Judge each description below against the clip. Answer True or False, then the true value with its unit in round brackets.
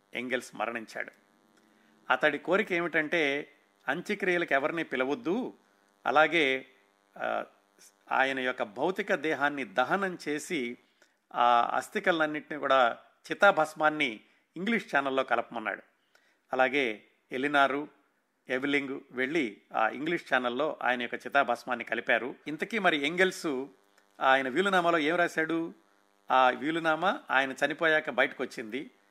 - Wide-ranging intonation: False (4.5 semitones)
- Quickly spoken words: False (95 wpm)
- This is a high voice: False (140 Hz)